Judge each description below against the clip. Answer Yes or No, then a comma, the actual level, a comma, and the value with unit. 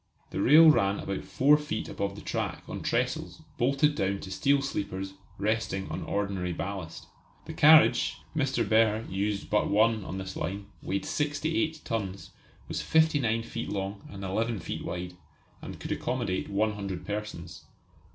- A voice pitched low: Yes, low, 105 Hz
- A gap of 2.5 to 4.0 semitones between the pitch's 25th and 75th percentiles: No, average, 4.6 semitones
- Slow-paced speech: No, average, 155 wpm